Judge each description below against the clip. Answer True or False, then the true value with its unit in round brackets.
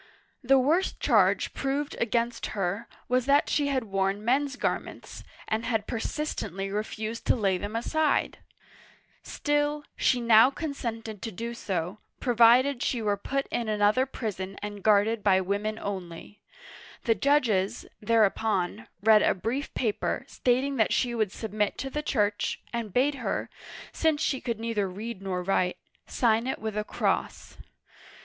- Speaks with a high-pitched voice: True (225 Hz)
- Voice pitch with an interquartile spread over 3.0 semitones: True (3.9 semitones)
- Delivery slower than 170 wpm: True (155 wpm)